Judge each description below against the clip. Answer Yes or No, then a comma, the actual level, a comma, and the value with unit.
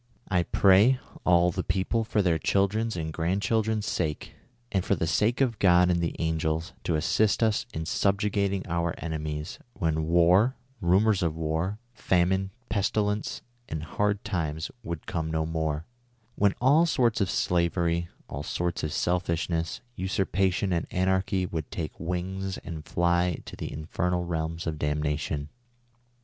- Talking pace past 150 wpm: No, average, 145 wpm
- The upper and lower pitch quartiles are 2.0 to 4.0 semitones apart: Yes, average, 3.5 semitones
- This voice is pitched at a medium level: No, very low, 90 Hz